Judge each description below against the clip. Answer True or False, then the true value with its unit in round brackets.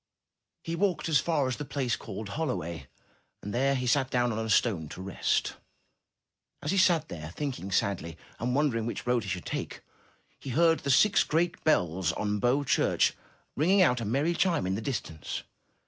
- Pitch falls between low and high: False (125 Hz)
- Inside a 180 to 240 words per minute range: True (185 wpm)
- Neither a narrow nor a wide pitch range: False (7.0 semitones)